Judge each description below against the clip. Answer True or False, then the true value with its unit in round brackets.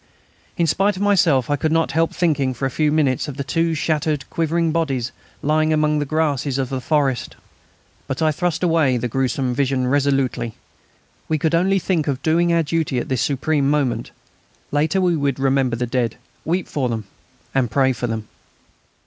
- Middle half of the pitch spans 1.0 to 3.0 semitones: False (3.6 semitones)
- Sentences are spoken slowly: False (185 wpm)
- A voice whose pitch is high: False (145 Hz)